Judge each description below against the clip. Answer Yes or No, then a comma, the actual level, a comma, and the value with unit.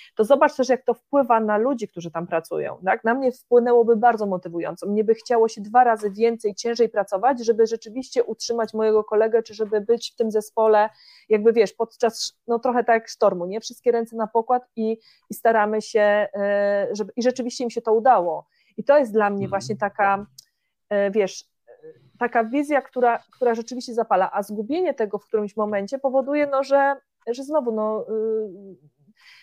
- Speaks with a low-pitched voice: No, high, 225 Hz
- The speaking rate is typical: No, fast, 175 wpm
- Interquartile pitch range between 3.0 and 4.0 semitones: No, narrow, 2.5 semitones